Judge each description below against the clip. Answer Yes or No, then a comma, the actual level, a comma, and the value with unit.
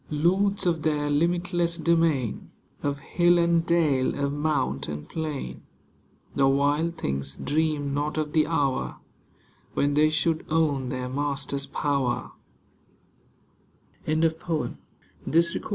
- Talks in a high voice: No, medium, 150 Hz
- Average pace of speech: No, slow, 105 wpm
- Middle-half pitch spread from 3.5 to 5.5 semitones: No, average, 2.9 semitones